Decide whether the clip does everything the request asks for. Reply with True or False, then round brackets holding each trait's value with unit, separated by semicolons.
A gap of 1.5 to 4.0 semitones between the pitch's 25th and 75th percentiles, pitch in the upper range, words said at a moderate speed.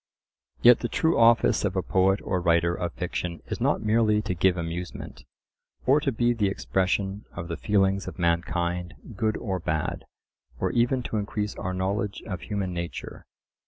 False (3.6 semitones; 95 Hz; 170 wpm)